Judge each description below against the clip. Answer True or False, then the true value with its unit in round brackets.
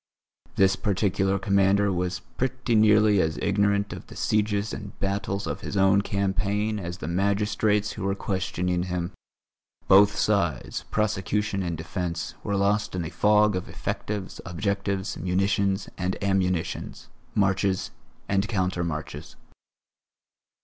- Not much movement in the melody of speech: True (2.1 semitones)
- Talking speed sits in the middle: False (130 wpm)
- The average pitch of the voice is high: False (100 Hz)